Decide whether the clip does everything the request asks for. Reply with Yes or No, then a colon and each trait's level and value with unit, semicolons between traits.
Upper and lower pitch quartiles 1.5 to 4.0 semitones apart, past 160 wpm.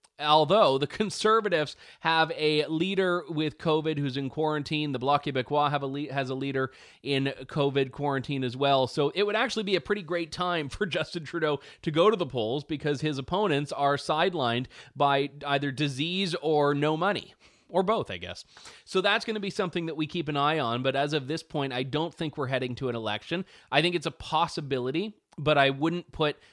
Yes: average, 3.4 semitones; fast, 205 wpm